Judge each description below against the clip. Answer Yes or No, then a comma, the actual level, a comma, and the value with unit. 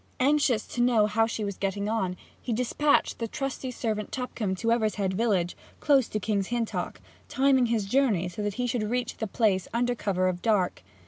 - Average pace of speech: Yes, average, 190 wpm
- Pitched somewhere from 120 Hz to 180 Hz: No, high, 225 Hz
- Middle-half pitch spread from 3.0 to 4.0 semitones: Yes, average, 3.6 semitones